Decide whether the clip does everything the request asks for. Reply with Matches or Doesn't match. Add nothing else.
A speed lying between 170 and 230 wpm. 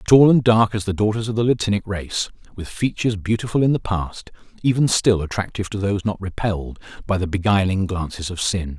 Matches